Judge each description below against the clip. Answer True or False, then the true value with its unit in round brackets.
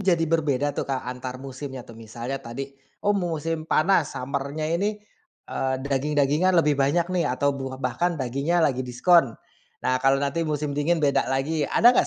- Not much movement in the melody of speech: False (3.7 semitones)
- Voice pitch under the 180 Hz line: True (140 Hz)